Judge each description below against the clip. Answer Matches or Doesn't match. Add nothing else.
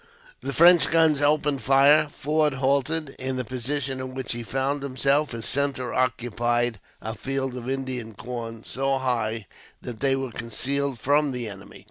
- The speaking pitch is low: Matches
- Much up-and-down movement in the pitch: Doesn't match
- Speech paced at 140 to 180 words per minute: Matches